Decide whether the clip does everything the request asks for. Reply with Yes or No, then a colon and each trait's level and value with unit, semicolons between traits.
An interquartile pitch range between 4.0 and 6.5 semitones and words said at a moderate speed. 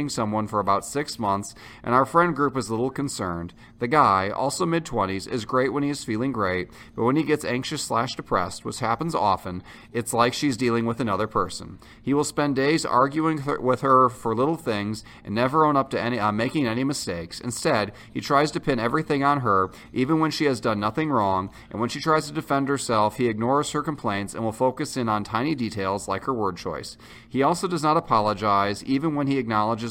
No: average, 4.9 semitones; fast, 220 wpm